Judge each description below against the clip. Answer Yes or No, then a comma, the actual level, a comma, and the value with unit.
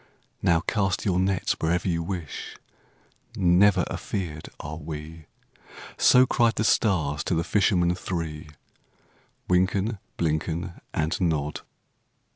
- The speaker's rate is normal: No, slow, 110 wpm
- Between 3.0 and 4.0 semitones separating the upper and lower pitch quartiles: Yes, average, 3.3 semitones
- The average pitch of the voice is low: Yes, very low, 85 Hz